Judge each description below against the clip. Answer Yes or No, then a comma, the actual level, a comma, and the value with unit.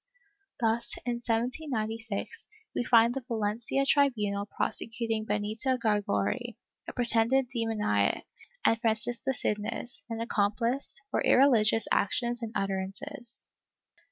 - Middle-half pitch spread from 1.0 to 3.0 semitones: Yes, narrow, 2.4 semitones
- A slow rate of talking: Yes, slow, 100 wpm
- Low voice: No, high, 230 Hz